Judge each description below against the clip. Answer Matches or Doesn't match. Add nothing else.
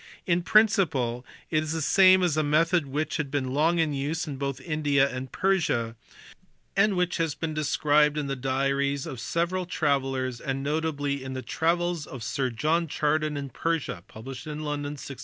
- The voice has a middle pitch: Matches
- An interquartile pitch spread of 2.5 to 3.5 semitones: Matches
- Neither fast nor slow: Matches